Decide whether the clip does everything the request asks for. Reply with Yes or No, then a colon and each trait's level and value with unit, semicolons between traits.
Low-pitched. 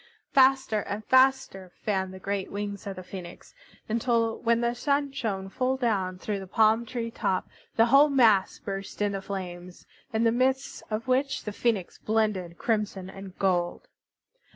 No: high, 215 Hz